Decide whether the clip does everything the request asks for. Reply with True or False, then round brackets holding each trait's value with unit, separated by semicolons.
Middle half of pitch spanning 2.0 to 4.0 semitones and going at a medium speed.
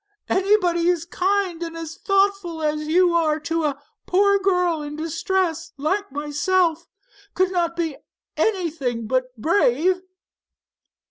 False (3.5 semitones; 120 wpm)